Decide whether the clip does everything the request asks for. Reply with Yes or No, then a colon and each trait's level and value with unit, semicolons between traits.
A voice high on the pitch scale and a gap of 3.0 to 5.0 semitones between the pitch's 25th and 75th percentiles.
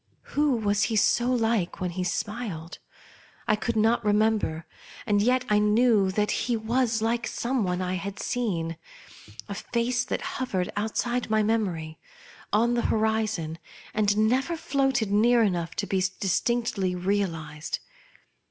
Yes: high, 215 Hz; average, 3.9 semitones